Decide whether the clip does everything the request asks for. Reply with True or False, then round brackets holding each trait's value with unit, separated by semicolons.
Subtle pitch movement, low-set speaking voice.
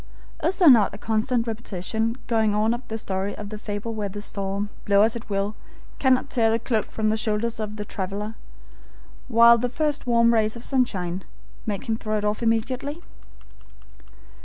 False (2.2 semitones; 220 Hz)